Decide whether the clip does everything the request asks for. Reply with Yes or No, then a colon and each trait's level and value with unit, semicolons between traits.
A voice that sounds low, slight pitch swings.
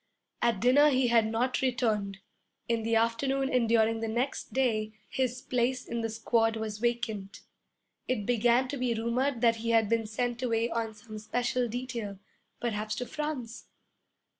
No: high, 235 Hz; narrow, 2.0 semitones